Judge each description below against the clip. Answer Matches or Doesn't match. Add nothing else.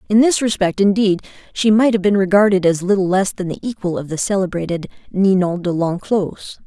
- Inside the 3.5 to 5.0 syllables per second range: Doesn't match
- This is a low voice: Doesn't match